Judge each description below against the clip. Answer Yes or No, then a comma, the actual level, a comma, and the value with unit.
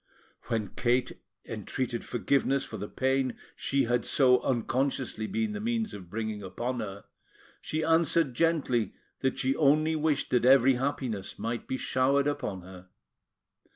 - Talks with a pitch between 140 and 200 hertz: No, low, 130 Hz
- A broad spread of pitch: No, average, 3.8 semitones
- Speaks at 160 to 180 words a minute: No, average, 145 wpm